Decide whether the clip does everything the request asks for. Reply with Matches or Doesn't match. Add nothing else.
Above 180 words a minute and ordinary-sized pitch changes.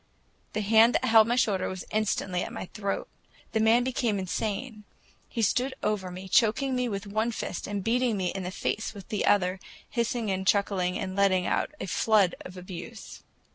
Matches